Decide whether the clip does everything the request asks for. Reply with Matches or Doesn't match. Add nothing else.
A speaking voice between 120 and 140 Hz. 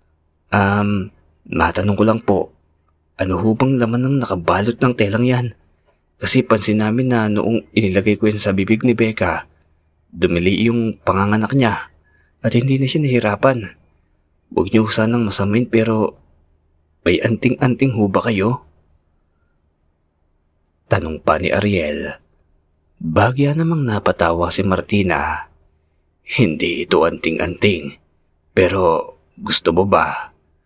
Doesn't match